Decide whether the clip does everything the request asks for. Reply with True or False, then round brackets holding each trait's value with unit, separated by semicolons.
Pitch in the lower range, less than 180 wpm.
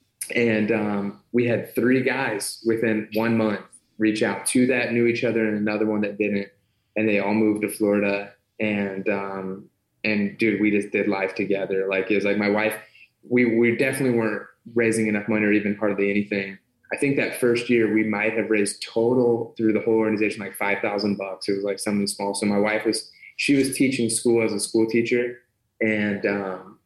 False (110 Hz; 200 wpm)